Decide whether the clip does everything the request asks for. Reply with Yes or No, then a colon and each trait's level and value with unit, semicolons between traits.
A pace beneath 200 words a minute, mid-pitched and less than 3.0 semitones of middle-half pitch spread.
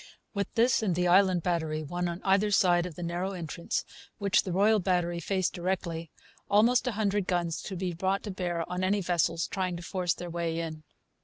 No: fast, 205 wpm; medium, 180 Hz; narrow, 2.4 semitones